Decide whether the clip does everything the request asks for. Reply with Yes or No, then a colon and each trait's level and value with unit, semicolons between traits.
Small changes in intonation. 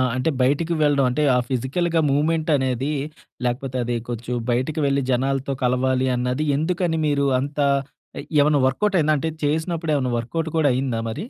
No: average, 3.6 semitones